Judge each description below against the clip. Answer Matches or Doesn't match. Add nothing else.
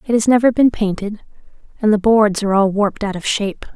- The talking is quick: Matches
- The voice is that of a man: Doesn't match